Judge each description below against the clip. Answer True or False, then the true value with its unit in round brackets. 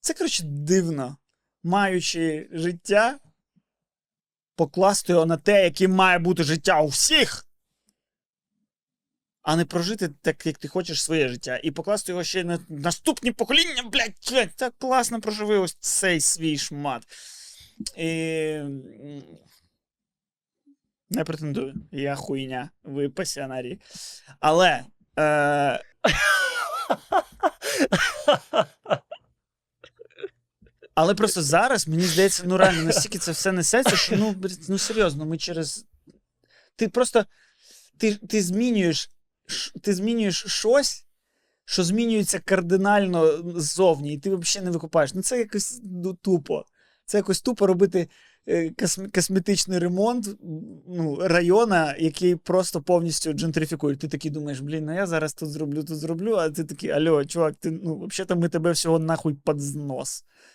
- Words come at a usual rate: True (120 wpm)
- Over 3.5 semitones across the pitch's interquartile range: True (4.3 semitones)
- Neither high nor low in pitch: True (180 Hz)